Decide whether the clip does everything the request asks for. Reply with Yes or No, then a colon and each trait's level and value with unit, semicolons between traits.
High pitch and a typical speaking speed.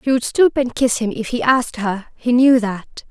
No: high, 240 Hz; fast, 250 wpm